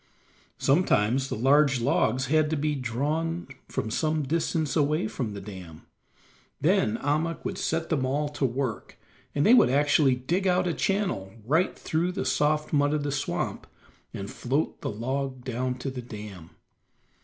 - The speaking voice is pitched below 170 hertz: Yes, medium, 140 Hz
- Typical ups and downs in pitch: Yes, average, 4.0 semitones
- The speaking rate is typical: Yes, average, 165 wpm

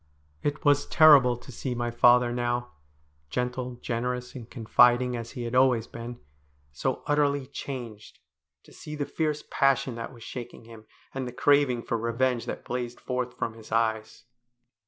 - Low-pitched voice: Yes, low, 125 Hz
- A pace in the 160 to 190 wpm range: Yes, average, 170 wpm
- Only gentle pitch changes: Yes, narrow, 2.0 semitones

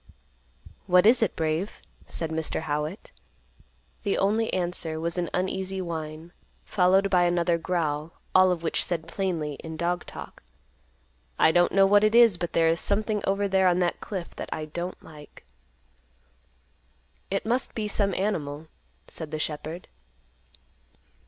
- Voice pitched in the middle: Yes, medium, 175 Hz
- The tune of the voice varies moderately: Yes, average, 3.3 semitones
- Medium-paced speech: Yes, average, 150 wpm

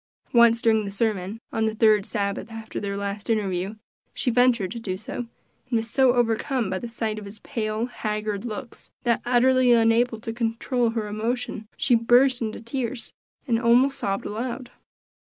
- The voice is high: Yes, high, 225 Hz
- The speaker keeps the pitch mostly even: Yes, narrow, 2.3 semitones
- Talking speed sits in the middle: Yes, average, 170 wpm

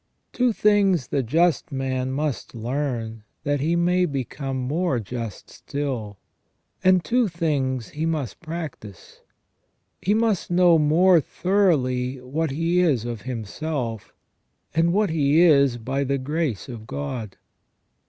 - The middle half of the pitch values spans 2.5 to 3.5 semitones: No, average, 5.2 semitones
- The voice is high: No, medium, 145 Hz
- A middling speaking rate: No, slow, 130 wpm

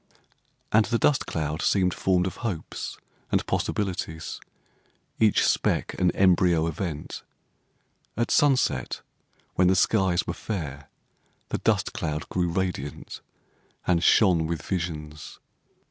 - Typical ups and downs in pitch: Yes, average, 3.3 semitones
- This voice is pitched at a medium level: No, very low, 90 Hz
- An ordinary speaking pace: No, slow, 115 wpm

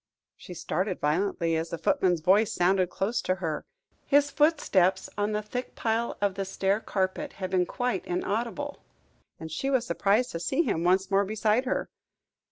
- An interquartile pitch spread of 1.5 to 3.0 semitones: No, average, 4.0 semitones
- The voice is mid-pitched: No, high, 195 Hz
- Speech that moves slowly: No, average, 175 wpm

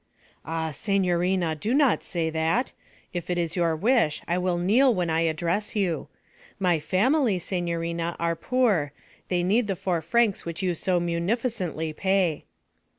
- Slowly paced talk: No, average, 150 wpm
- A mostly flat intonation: No, average, 3.2 semitones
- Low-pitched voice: No, medium, 175 Hz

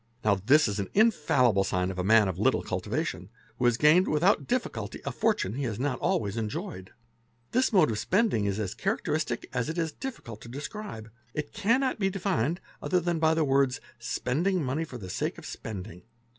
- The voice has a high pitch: No, low, 135 Hz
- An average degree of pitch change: No, wide, 8.7 semitones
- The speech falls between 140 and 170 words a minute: No, average, 195 wpm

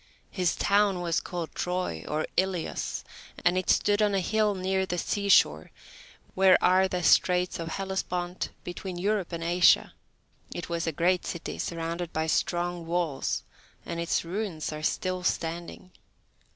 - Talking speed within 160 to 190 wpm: No, average, 150 wpm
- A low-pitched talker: No, medium, 180 Hz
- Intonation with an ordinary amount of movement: No, narrow, 2.1 semitones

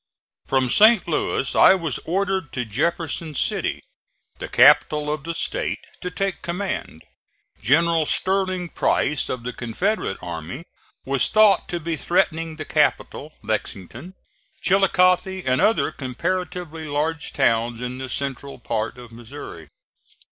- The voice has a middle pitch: Yes, medium, 155 Hz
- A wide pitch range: Yes, wide, 6.3 semitones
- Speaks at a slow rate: Yes, slow, 130 wpm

